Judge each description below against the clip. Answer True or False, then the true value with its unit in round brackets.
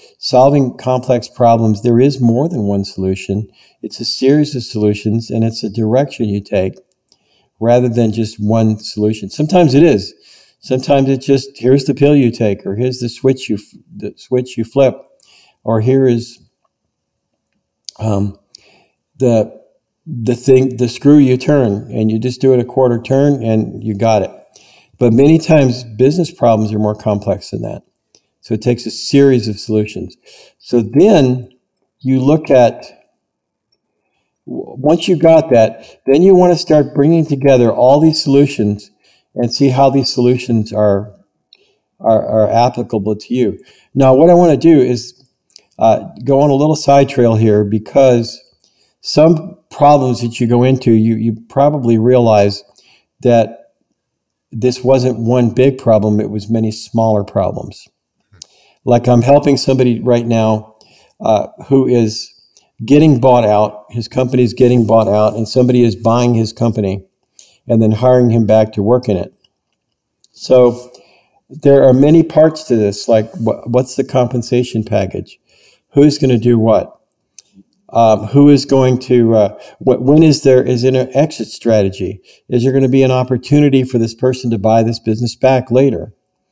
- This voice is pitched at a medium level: False (125 Hz)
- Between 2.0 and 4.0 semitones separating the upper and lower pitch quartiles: True (3.4 semitones)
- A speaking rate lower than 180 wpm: True (160 wpm)